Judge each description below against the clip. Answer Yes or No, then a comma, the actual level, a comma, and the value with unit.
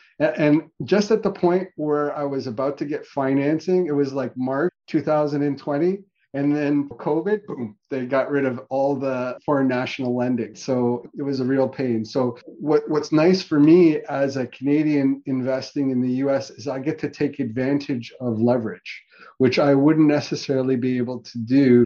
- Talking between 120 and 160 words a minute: No, average, 180 wpm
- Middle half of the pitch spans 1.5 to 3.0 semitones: Yes, average, 2.7 semitones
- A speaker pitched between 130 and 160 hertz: Yes, medium, 140 Hz